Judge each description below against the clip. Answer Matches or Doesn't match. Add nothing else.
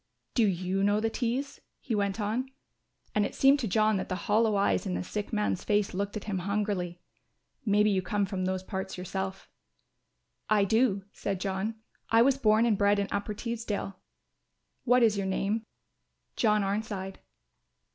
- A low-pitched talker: Doesn't match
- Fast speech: Doesn't match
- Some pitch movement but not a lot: Doesn't match